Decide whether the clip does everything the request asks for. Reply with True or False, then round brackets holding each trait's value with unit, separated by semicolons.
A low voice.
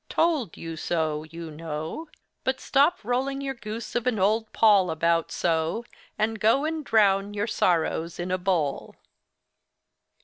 False (200 Hz)